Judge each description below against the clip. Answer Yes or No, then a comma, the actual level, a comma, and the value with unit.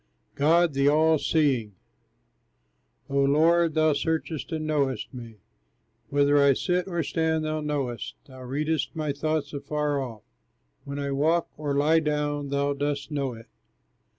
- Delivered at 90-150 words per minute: Yes, average, 145 wpm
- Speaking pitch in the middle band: Yes, medium, 145 Hz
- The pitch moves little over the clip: Yes, narrow, 2.1 semitones